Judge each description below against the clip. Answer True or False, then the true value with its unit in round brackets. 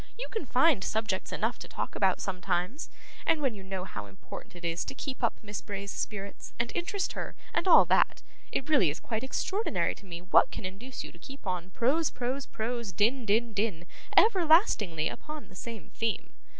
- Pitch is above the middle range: True (220 Hz)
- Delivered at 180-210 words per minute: True (195 wpm)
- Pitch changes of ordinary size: False (6.3 semitones)